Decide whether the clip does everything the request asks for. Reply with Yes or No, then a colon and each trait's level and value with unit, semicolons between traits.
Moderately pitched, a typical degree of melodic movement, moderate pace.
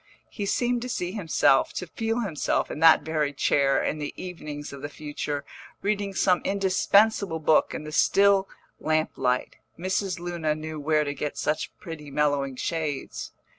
Yes: medium, 160 Hz; average, 4.6 semitones; average, 165 wpm